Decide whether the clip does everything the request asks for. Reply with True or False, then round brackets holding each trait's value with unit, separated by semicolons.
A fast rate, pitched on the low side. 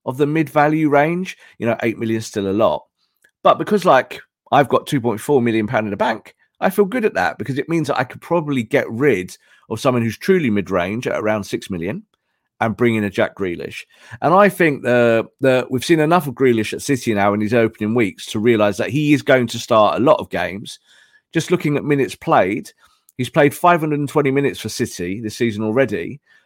True (215 wpm; 130 Hz)